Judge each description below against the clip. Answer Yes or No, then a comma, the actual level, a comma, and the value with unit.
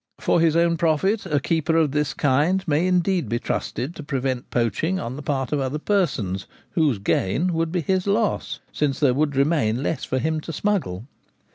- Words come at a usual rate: Yes, average, 190 wpm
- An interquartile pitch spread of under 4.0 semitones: No, average, 4.3 semitones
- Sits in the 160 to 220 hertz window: No, medium, 150 Hz